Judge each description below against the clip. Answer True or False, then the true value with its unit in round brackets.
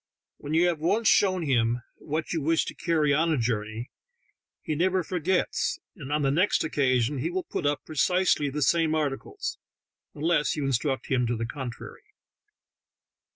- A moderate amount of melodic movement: True (4.1 semitones)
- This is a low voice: False (150 Hz)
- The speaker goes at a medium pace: True (165 wpm)